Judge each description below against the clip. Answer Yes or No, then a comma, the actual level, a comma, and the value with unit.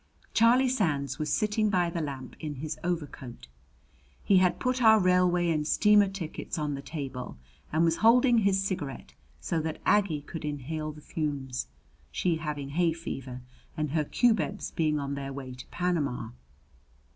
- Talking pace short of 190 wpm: Yes, average, 160 wpm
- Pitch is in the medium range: Yes, medium, 160 Hz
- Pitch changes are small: No, average, 4.9 semitones